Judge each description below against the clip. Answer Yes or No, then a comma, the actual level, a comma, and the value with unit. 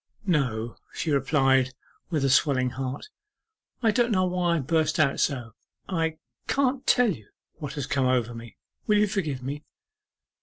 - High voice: No, medium, 145 Hz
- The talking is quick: No, average, 155 wpm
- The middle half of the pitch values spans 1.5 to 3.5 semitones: No, wide, 5.6 semitones